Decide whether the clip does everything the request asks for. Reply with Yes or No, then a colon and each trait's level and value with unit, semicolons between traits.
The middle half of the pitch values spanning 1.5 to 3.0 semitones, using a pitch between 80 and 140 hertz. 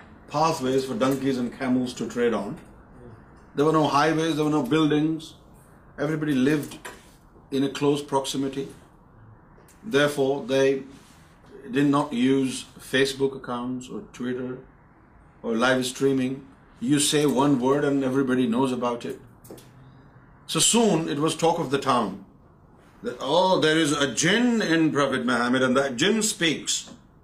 Yes: narrow, 2.5 semitones; low, 135 Hz